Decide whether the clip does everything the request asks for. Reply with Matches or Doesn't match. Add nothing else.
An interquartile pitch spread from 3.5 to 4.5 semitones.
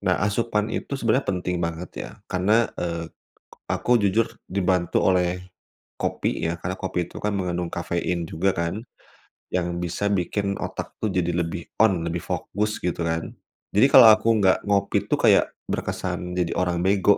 Doesn't match